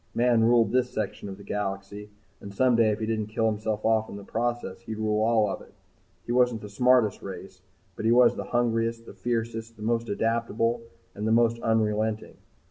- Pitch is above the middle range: No, low, 110 Hz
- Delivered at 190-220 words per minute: Yes, average, 200 wpm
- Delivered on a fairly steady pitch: Yes, narrow, 1.8 semitones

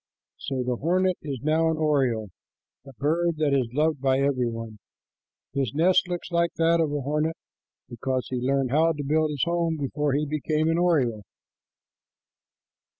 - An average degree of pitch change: Yes, average, 3.6 semitones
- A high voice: No, medium, 150 Hz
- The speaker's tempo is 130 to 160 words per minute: No, average, 170 wpm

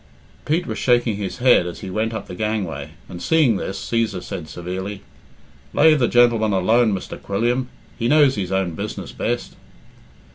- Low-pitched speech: Yes, low, 110 Hz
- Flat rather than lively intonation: No, average, 4.5 semitones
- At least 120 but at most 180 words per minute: Yes, average, 170 wpm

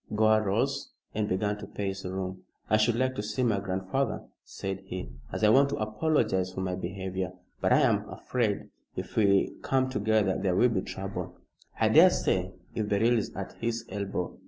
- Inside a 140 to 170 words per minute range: No, average, 185 wpm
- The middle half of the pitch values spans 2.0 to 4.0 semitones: Yes, average, 2.8 semitones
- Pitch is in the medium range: No, low, 105 Hz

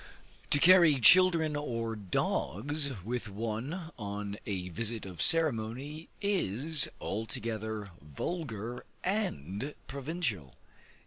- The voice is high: No, low, 115 Hz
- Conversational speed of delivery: No, slow, 90 wpm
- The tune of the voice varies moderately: No, wide, 7.1 semitones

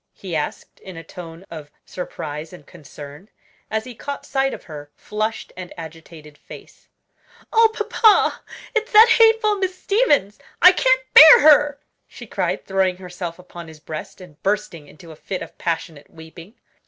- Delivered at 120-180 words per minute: Yes, average, 160 wpm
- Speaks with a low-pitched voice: No, medium, 185 Hz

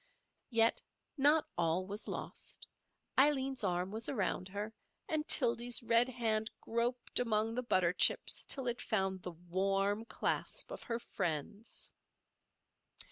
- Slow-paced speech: Yes, slow, 130 wpm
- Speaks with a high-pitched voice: Yes, high, 225 Hz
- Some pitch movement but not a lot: Yes, average, 4.2 semitones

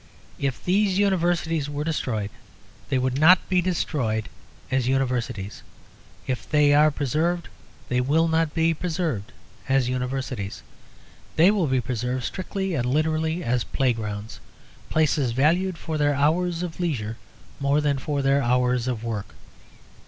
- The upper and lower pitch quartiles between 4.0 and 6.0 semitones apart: Yes, average, 4.6 semitones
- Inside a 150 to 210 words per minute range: No, average, 140 wpm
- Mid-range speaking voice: Yes, medium, 145 Hz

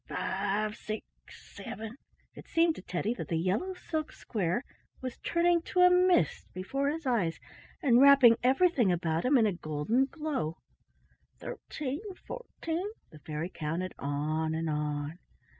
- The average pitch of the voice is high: Yes, high, 220 Hz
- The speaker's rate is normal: No, slow, 130 wpm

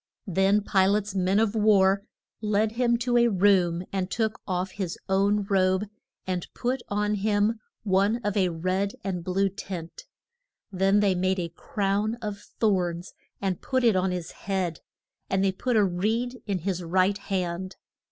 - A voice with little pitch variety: Yes, narrow, 2.1 semitones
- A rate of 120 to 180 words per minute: Yes, average, 165 wpm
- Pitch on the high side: Yes, high, 195 Hz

